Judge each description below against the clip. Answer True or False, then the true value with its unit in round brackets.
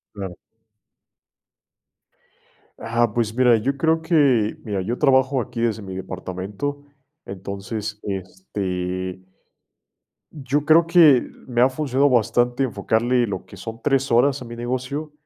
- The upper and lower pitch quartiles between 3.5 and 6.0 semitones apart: True (5.2 semitones)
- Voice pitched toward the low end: True (120 Hz)